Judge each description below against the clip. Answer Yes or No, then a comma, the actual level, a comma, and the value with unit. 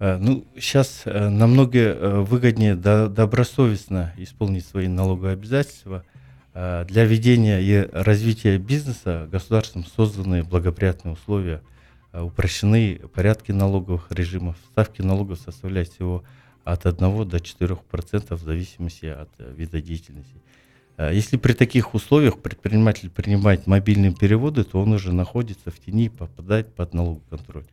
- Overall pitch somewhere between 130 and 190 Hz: No, low, 100 Hz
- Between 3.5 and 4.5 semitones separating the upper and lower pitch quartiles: Yes, average, 3.8 semitones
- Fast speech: No, average, 115 wpm